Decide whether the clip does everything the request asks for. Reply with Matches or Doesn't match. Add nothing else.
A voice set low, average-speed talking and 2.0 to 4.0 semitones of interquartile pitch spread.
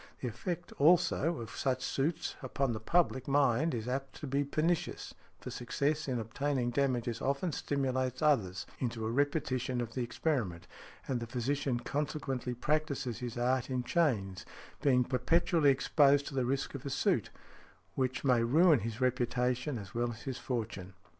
Matches